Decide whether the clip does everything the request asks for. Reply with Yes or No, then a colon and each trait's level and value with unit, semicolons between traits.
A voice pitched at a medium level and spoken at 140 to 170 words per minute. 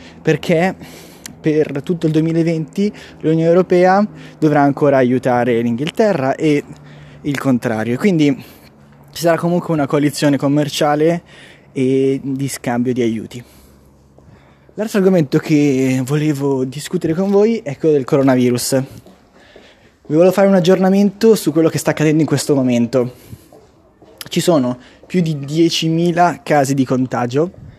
No: medium, 150 Hz; average, 125 wpm